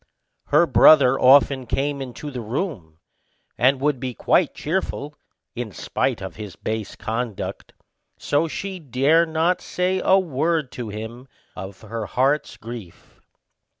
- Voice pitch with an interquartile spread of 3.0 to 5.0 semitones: No, wide, 5.4 semitones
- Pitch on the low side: Yes, low, 130 Hz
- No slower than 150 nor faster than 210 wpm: No, slow, 135 wpm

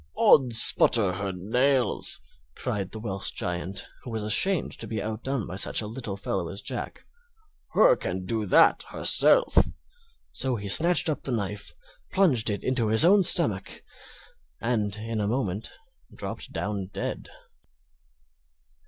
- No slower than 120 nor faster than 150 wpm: Yes, average, 145 wpm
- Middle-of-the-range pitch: No, low, 110 Hz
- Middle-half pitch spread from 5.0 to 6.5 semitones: No, average, 4.6 semitones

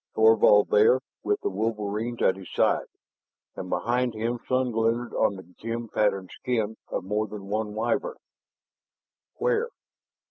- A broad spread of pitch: No, average, 2.7 semitones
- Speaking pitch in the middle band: No, low, 110 Hz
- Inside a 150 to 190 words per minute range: No, average, 140 wpm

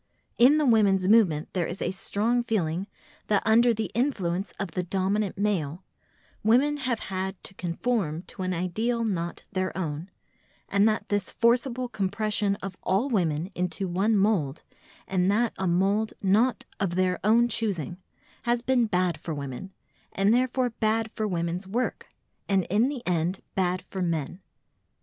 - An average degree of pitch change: Yes, average, 3.8 semitones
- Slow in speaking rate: No, average, 155 wpm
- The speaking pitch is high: Yes, high, 195 Hz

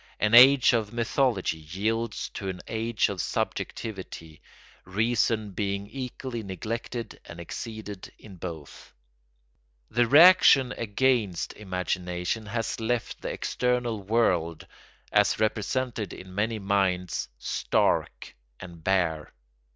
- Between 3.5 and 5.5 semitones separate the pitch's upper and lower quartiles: Yes, average, 4.1 semitones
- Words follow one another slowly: Yes, slow, 105 wpm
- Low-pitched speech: Yes, low, 105 Hz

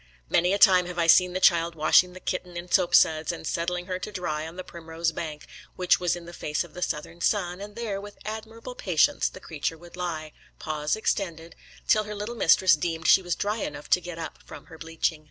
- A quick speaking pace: Yes, fast, 225 wpm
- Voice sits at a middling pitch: Yes, medium, 175 Hz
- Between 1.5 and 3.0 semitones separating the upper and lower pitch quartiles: Yes, narrow, 2.4 semitones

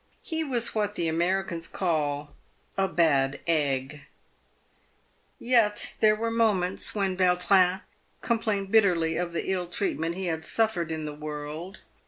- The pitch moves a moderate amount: Yes, average, 4.4 semitones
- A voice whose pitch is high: No, medium, 180 Hz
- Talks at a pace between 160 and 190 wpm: No, average, 145 wpm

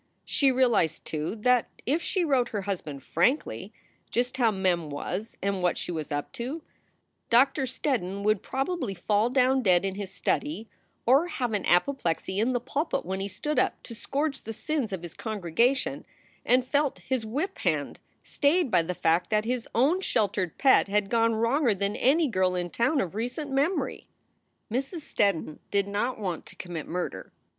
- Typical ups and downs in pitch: No, wide, 6.0 semitones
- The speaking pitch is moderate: No, high, 225 Hz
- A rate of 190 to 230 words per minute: No, average, 175 wpm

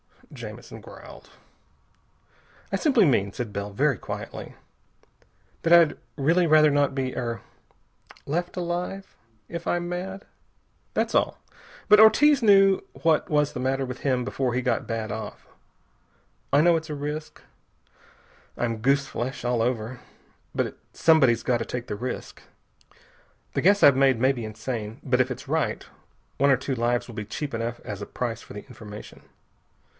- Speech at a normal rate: Yes, average, 160 wpm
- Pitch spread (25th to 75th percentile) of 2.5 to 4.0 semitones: No, wide, 5.5 semitones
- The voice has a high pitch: No, low, 135 Hz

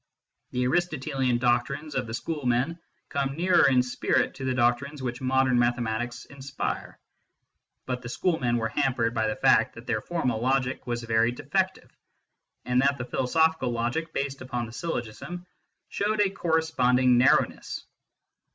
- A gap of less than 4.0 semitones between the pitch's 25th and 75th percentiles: Yes, average, 2.8 semitones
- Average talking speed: Yes, average, 145 wpm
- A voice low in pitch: Yes, low, 130 Hz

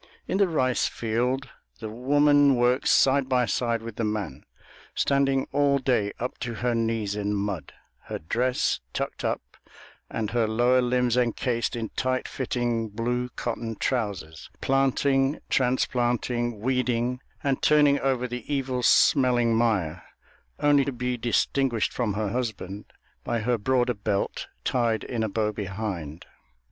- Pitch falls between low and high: No, low, 120 Hz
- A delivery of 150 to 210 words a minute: No, average, 140 wpm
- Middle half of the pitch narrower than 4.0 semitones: Yes, average, 2.7 semitones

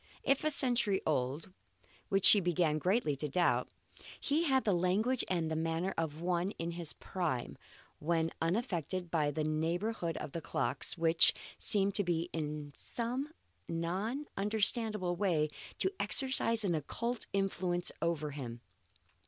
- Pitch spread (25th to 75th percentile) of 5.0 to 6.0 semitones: No, average, 4.6 semitones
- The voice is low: No, medium, 175 Hz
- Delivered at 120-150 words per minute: Yes, slow, 135 wpm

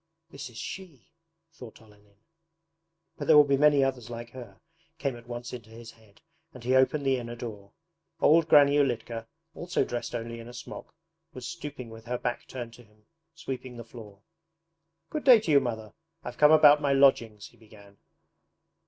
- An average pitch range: Yes, average, 3.7 semitones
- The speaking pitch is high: No, low, 120 Hz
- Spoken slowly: No, average, 180 wpm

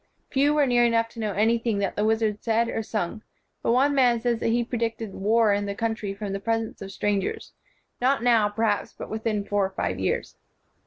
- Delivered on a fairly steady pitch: Yes, narrow, 2.2 semitones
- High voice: Yes, high, 225 Hz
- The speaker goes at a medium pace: No, fast, 210 wpm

